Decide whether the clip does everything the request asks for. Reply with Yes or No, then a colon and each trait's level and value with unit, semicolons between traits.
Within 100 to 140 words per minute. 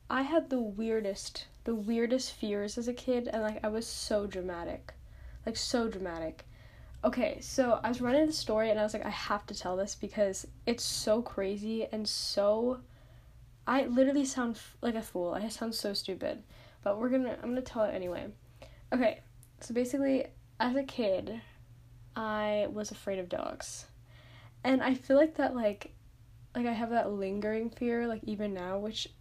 No: average, 180 wpm